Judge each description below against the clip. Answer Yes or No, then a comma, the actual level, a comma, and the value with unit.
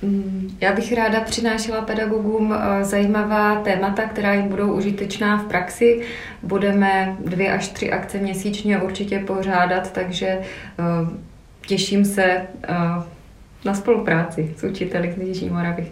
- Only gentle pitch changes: Yes, narrow, 2.2 semitones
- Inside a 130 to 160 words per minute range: No, slow, 115 wpm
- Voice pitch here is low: No, high, 195 Hz